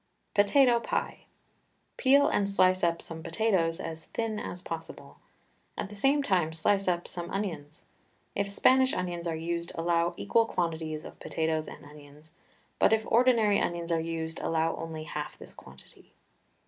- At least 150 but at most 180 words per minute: Yes, average, 155 wpm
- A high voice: No, medium, 170 Hz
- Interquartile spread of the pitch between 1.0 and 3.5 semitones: No, average, 4.1 semitones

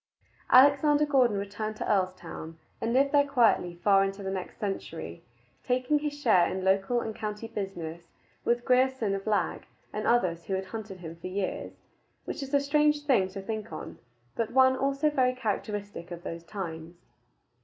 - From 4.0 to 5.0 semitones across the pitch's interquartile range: No, wide, 5.5 semitones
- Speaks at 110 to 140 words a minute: No, average, 170 wpm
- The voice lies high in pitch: Yes, high, 210 Hz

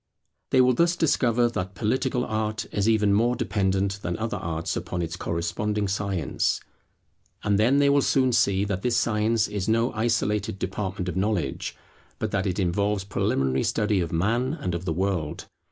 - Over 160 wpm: Yes, average, 170 wpm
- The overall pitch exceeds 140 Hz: No, low, 105 Hz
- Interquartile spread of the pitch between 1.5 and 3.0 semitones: No, average, 3.6 semitones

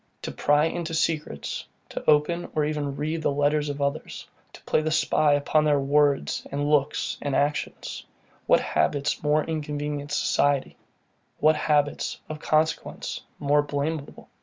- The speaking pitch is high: No, medium, 150 Hz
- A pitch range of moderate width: No, narrow, 1.2 semitones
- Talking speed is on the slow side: No, average, 150 wpm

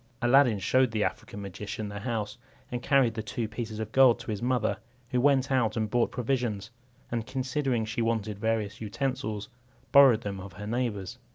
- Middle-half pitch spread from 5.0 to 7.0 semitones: No, average, 3.3 semitones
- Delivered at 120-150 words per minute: No, average, 180 wpm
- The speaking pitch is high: No, low, 115 Hz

